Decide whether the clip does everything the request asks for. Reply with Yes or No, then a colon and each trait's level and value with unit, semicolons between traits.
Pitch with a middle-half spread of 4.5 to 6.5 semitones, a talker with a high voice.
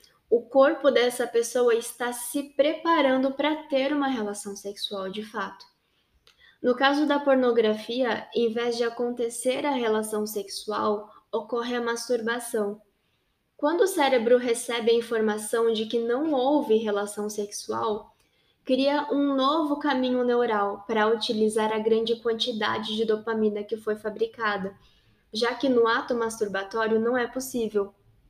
No: average, 3.2 semitones; high, 235 Hz